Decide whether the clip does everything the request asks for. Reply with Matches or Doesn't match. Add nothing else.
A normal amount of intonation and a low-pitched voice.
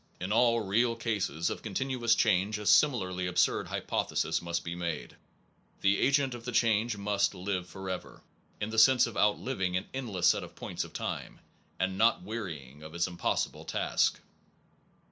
Matches